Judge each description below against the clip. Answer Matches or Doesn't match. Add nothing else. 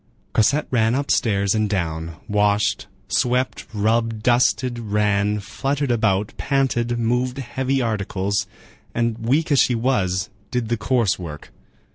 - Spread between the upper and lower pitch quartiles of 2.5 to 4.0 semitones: Matches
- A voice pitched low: Matches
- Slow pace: Matches